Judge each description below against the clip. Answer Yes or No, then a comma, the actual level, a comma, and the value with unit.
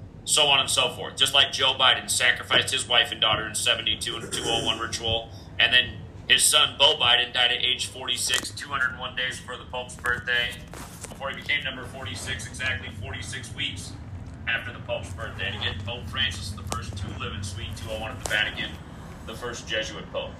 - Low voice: Yes, low, 110 Hz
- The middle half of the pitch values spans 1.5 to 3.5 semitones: No, average, 3.9 semitones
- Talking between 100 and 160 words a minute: No, average, 195 wpm